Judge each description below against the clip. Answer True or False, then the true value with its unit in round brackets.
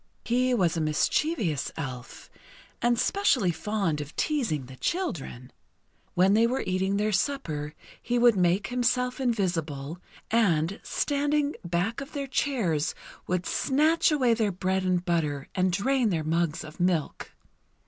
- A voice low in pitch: False (190 Hz)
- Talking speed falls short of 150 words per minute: True (140 wpm)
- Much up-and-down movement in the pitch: True (7.3 semitones)